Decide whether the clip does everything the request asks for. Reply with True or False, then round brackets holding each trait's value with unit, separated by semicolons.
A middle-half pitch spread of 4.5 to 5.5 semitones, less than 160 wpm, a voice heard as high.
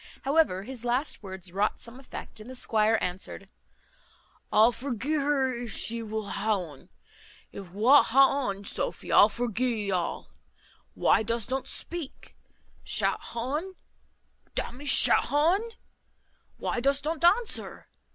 True (4.9 semitones; 150 wpm; 240 Hz)